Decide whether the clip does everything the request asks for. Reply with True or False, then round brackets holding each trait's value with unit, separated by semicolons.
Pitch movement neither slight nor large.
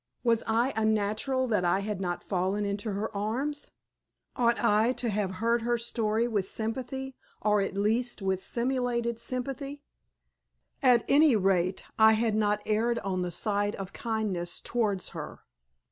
True (3.0 semitones)